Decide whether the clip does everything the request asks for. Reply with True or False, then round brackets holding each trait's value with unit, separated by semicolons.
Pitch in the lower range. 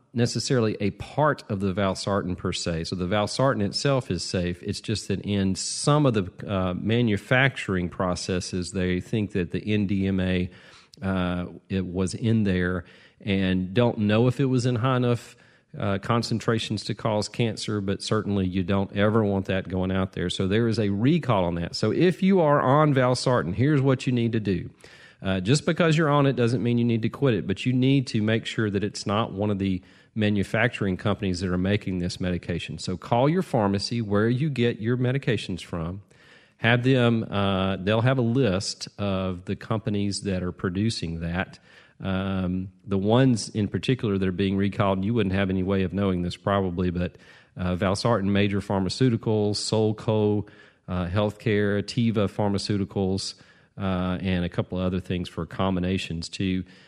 True (100 Hz)